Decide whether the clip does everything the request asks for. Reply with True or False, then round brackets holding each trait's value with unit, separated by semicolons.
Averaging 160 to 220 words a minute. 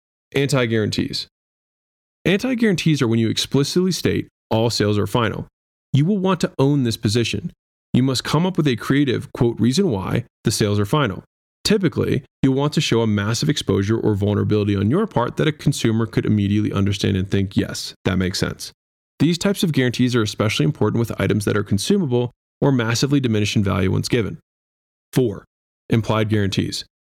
True (175 wpm)